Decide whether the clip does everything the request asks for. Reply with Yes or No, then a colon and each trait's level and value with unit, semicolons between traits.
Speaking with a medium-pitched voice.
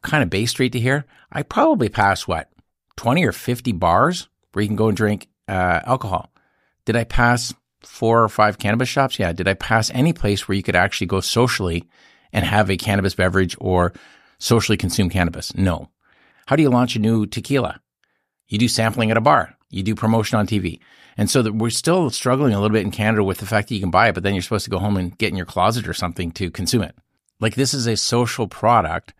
No: low, 105 Hz